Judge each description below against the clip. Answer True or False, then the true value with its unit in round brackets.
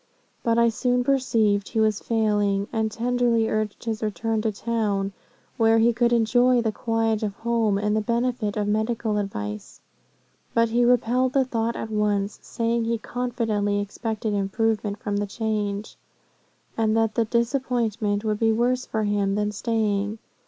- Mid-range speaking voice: False (220 Hz)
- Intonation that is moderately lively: False (2.0 semitones)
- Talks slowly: False (160 wpm)